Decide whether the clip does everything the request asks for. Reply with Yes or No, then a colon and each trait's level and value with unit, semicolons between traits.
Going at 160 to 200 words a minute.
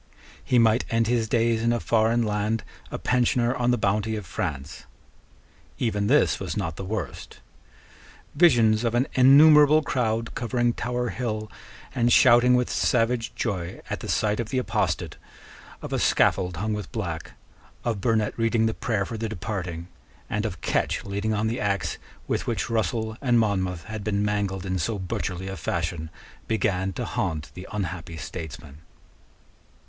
Yes: average, 165 wpm